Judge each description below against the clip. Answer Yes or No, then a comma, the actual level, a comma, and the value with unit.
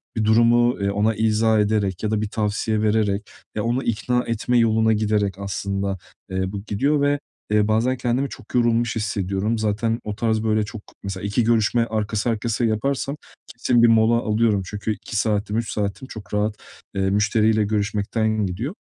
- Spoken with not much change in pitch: Yes, narrow, 2.0 semitones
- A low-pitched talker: Yes, low, 110 Hz